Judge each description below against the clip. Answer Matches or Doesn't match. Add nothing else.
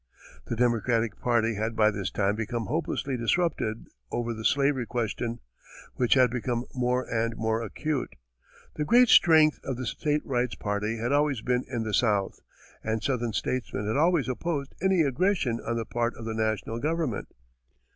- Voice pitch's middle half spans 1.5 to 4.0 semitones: Matches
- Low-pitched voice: Matches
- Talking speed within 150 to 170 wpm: Matches